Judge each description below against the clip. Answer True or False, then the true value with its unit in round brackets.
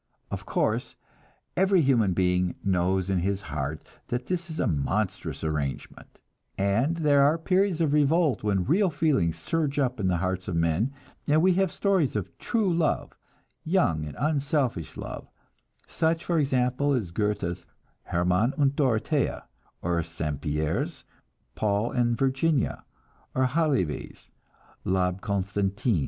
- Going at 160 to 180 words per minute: False (140 wpm)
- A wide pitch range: True (8.8 semitones)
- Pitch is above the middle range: False (120 Hz)